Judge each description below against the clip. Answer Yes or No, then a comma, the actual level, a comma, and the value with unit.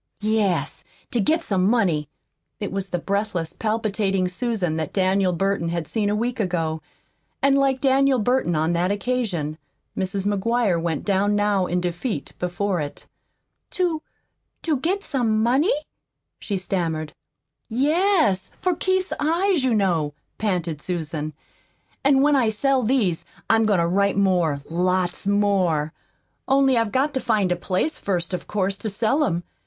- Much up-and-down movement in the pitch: Yes, wide, 6.0 semitones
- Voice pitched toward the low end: No, high, 200 Hz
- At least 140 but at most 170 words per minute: Yes, average, 150 wpm